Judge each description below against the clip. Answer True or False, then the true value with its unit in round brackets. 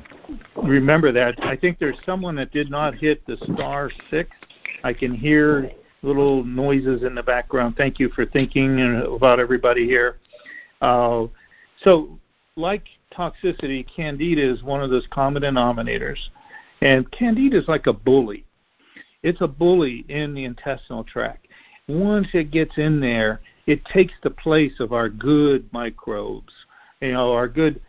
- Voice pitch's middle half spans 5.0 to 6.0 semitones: False (3.7 semitones)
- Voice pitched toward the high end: False (140 Hz)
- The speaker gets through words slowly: False (150 wpm)